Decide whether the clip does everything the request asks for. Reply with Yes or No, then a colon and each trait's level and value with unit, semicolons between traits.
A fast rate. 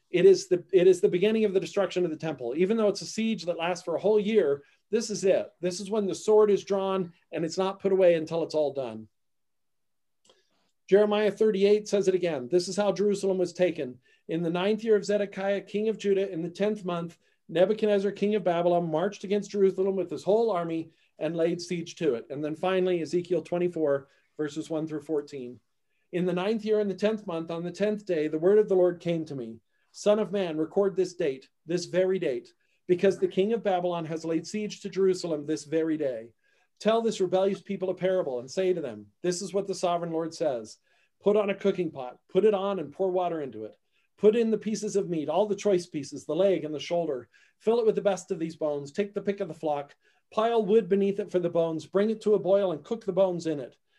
Yes: fast, 235 wpm